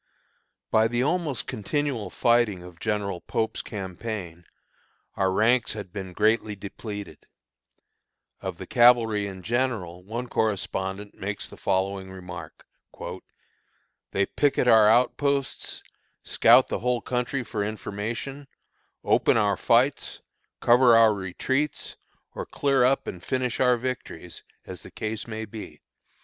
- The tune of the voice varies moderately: Yes, average, 3.9 semitones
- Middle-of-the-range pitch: No, low, 110 Hz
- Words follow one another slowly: Yes, slow, 125 wpm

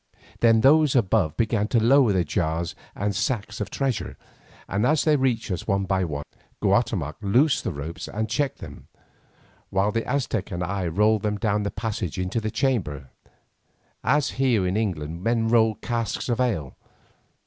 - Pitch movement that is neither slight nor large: Yes, average, 4.4 semitones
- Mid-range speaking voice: No, low, 105 Hz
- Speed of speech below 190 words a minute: Yes, average, 170 wpm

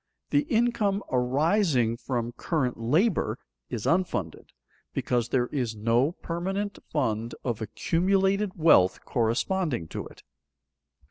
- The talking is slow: Yes, slow, 110 wpm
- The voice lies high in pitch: No, medium, 140 Hz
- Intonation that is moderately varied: No, wide, 8.4 semitones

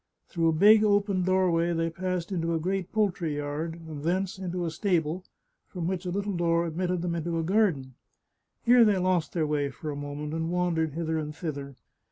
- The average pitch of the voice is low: No, medium, 170 Hz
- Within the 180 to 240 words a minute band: Yes, average, 200 wpm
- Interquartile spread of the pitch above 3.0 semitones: No, average, 2.7 semitones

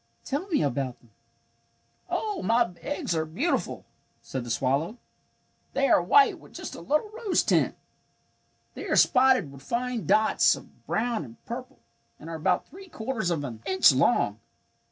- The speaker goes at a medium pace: Yes, average, 160 wpm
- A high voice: Yes, high, 220 Hz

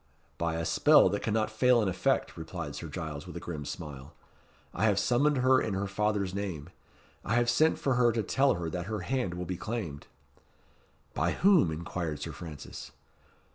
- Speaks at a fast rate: No, average, 185 wpm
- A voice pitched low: Yes, very low, 95 Hz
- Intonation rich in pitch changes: Yes, wide, 6.1 semitones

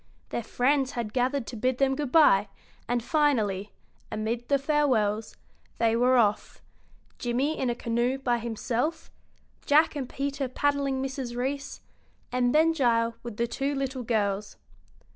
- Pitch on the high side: Yes, very high, 250 Hz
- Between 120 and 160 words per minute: Yes, average, 145 wpm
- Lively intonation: No, average, 3.2 semitones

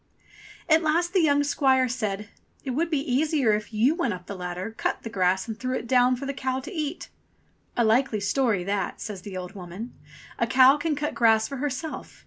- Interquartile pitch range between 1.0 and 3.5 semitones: No, wide, 5.5 semitones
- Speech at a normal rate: No, fast, 210 wpm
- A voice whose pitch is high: Yes, very high, 255 Hz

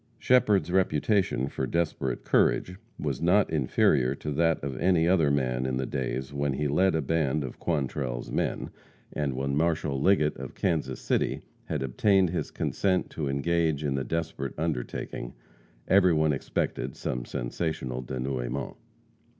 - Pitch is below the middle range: Yes, very low, 75 Hz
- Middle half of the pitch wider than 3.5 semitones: Yes, average, 4.1 semitones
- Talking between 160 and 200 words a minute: No, average, 145 wpm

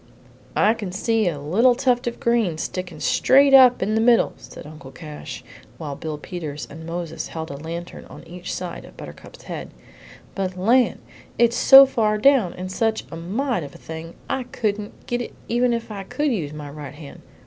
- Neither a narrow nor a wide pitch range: No, wide, 6.7 semitones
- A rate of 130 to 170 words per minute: No, average, 190 wpm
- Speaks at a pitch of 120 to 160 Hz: No, high, 195 Hz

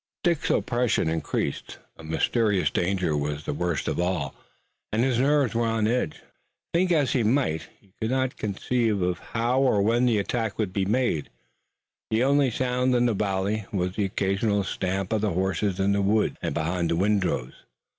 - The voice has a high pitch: No, low, 105 Hz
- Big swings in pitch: No, average, 4.8 semitones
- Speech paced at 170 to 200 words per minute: Yes, average, 175 wpm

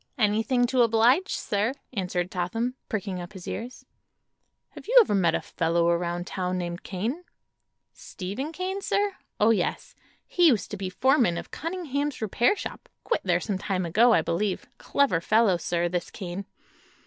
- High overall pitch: Yes, high, 210 Hz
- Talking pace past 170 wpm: No, average, 160 wpm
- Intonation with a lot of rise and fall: Yes, wide, 6.0 semitones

